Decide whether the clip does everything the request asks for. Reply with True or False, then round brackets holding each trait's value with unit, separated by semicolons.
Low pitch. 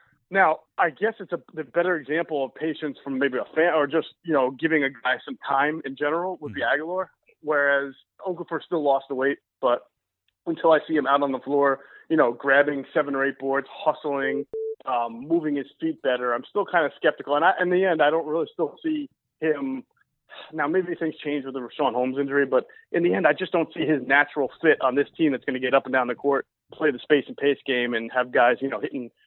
False (145 Hz)